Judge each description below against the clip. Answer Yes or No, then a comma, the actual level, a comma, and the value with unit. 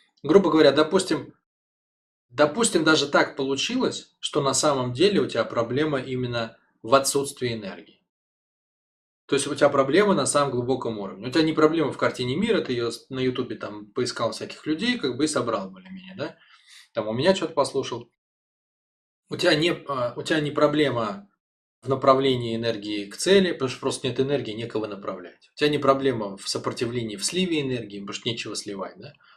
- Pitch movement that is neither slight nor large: Yes, average, 4.4 semitones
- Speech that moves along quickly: Yes, fast, 175 wpm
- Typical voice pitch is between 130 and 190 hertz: Yes, low, 135 Hz